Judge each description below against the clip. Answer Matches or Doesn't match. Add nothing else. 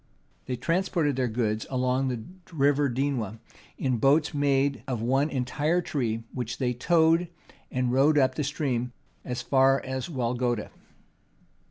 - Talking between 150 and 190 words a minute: Doesn't match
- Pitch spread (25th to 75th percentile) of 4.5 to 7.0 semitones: Doesn't match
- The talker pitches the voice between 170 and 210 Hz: Doesn't match